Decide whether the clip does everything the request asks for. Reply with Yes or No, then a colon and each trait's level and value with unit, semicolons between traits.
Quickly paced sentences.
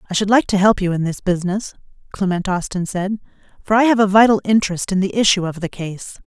Yes: fast, 230 wpm